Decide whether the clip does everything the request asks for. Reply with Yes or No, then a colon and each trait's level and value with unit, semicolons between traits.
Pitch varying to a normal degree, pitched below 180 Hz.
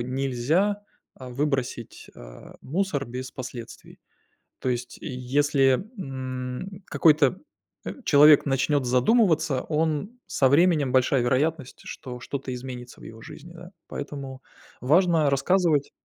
Yes: average, 3.8 semitones; low, 135 Hz